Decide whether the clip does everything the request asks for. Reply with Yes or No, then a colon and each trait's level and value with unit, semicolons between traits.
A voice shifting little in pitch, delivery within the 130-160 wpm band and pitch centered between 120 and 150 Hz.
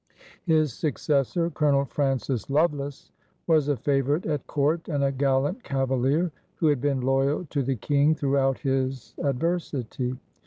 Yes: narrow, 2.2 semitones; average, 140 wpm; medium, 140 Hz